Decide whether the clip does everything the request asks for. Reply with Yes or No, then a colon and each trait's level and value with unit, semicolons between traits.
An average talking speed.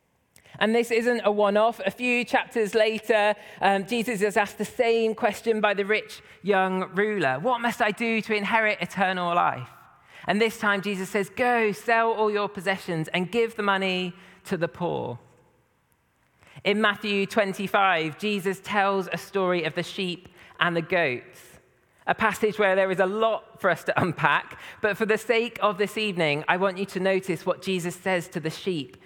Yes: average, 185 wpm